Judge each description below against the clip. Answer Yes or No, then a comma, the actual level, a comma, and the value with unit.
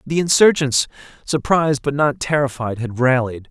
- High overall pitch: No, medium, 140 Hz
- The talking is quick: No, slow, 135 wpm